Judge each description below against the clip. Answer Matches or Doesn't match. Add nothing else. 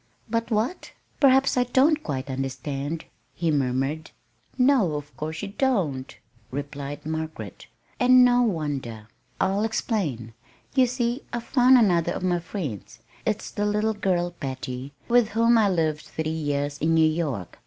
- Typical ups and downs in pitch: Doesn't match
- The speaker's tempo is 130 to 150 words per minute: Matches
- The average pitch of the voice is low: Doesn't match